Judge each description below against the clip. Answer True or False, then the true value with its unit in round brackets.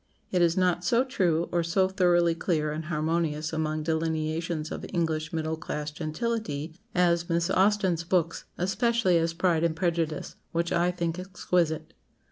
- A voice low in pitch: False (170 Hz)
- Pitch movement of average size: False (2.2 semitones)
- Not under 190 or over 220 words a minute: False (150 wpm)